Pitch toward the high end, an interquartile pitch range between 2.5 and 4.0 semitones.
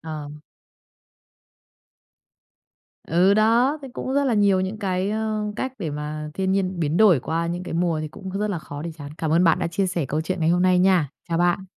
No: medium, 180 Hz; average, 3.7 semitones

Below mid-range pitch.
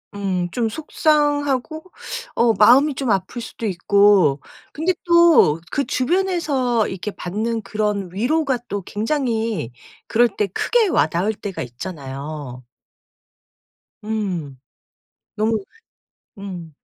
No: high, 215 Hz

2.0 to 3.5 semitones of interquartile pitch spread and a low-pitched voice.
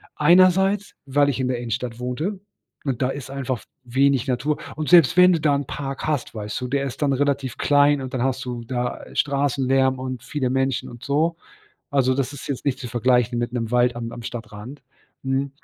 Yes: narrow, 2.5 semitones; low, 130 Hz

